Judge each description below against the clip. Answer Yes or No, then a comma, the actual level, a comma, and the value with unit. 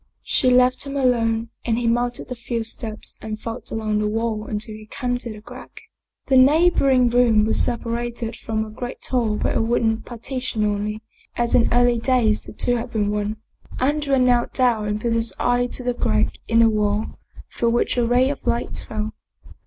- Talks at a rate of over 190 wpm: Yes, average, 200 wpm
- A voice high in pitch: Yes, high, 235 Hz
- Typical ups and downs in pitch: No, narrow, 2.2 semitones